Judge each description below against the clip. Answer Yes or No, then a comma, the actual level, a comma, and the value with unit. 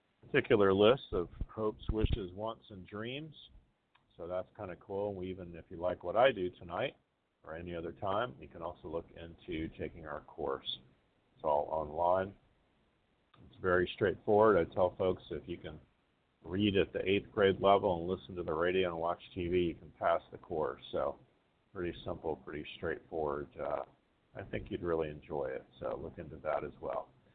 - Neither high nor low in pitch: No, very low, 90 Hz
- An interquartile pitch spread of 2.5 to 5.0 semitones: Yes, average, 2.9 semitones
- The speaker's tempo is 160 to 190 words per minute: Yes, average, 180 wpm